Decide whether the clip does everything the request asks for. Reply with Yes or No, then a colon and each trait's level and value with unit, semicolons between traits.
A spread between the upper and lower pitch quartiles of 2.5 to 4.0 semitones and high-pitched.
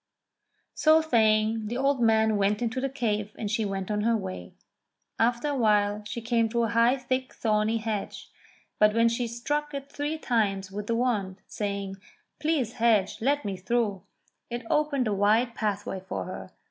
Yes: average, 3.0 semitones; high, 225 Hz